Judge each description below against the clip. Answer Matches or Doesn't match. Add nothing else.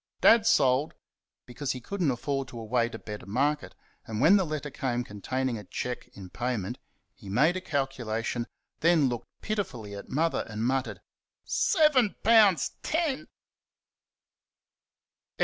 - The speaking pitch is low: Matches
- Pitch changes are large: Matches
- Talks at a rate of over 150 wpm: Doesn't match